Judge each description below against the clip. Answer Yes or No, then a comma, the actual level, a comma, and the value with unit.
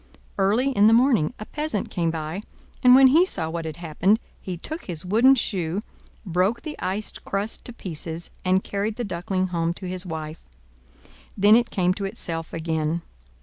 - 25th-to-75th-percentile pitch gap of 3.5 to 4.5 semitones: No, average, 4.9 semitones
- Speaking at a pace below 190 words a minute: Yes, average, 180 wpm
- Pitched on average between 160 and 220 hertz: Yes, medium, 185 Hz